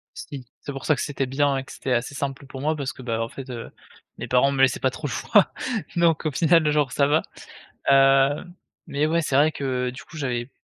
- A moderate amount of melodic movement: No, narrow, 2.3 semitones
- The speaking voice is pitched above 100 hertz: Yes, low, 135 Hz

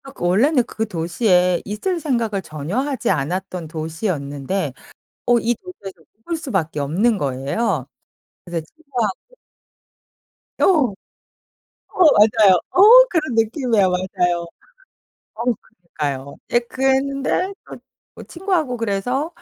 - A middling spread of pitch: No, wide, 7.2 semitones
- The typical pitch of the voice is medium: No, high, 210 Hz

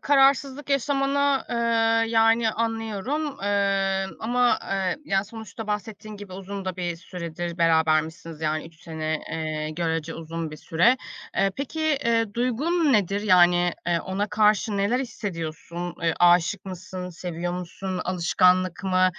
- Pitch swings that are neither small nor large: Yes, average, 4.8 semitones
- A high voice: Yes, high, 195 Hz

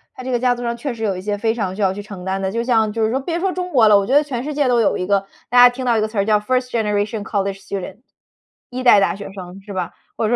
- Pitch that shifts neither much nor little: Yes, average, 3.7 semitones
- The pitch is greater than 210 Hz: Yes, high, 220 Hz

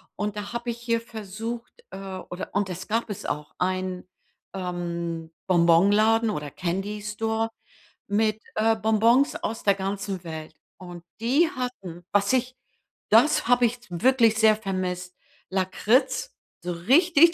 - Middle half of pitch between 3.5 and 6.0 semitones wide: Yes, average, 4.1 semitones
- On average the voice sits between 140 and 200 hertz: No, high, 210 Hz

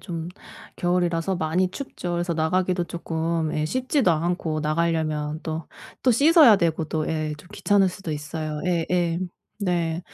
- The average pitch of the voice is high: No, medium, 170 Hz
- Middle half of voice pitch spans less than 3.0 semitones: Yes, narrow, 2.4 semitones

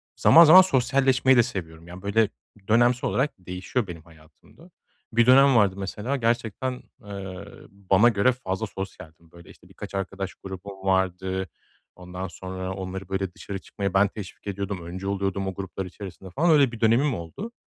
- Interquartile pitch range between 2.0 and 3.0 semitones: No, average, 4.2 semitones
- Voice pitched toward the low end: Yes, low, 100 Hz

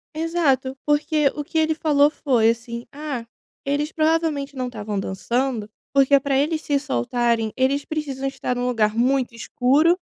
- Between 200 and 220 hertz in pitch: No, very high, 275 Hz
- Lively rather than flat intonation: No, average, 3.8 semitones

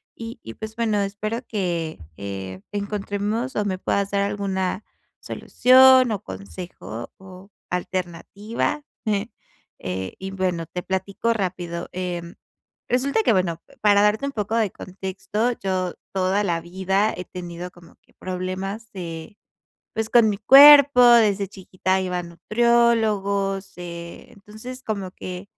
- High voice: Yes, high, 195 Hz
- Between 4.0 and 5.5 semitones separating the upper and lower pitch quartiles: No, average, 3.3 semitones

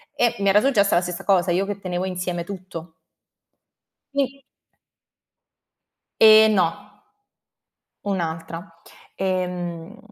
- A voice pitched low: No, medium, 185 Hz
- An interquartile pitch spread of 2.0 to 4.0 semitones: Yes, average, 2.7 semitones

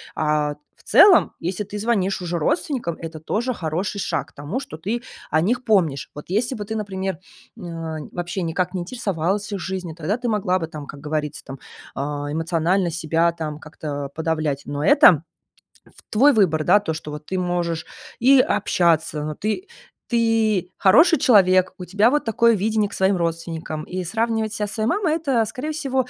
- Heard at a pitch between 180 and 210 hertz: Yes, medium, 185 Hz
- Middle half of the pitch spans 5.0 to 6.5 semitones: Yes, average, 5.3 semitones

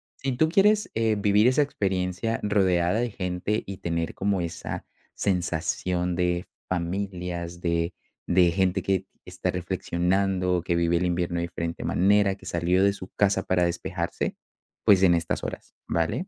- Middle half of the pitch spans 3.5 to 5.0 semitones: No, narrow, 2.4 semitones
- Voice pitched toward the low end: Yes, very low, 90 Hz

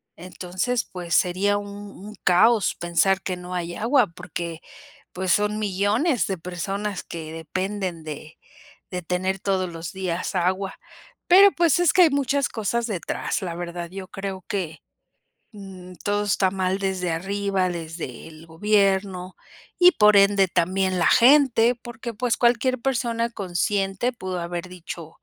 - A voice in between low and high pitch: No, high, 195 Hz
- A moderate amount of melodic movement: Yes, average, 3.0 semitones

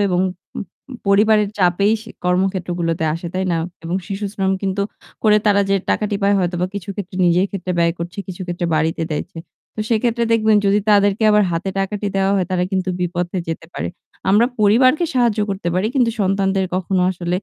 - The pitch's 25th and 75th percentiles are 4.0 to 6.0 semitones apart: No, narrow, 2.6 semitones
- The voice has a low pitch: No, high, 195 Hz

